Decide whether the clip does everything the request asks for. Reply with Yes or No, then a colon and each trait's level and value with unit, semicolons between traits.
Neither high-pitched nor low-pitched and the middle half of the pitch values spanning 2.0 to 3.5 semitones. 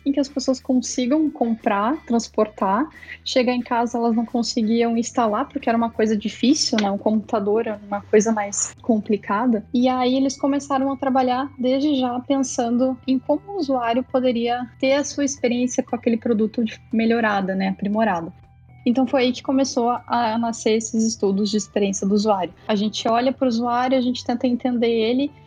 No: high, 240 Hz; average, 2.8 semitones